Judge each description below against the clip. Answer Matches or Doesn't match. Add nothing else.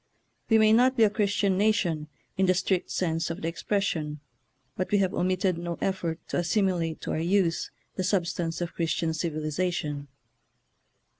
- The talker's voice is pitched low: Doesn't match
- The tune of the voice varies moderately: Matches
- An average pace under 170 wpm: Doesn't match